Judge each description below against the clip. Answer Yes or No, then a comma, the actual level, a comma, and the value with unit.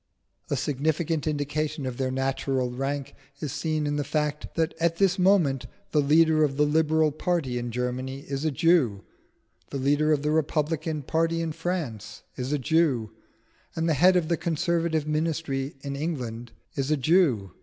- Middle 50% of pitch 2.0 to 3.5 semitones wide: Yes, average, 3.2 semitones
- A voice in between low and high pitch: Yes, medium, 150 Hz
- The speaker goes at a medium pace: Yes, average, 170 wpm